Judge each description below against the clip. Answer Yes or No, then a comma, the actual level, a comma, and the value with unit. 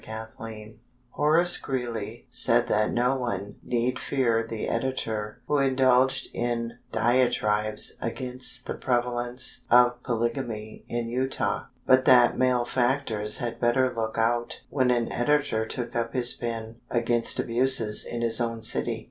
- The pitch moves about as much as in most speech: No, narrow, 2.0 semitones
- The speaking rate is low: Yes, slow, 130 wpm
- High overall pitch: No, low, 120 Hz